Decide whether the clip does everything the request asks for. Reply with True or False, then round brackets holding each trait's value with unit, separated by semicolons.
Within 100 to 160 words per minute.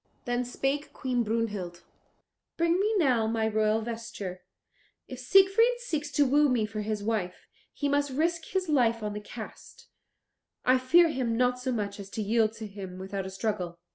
False (175 wpm)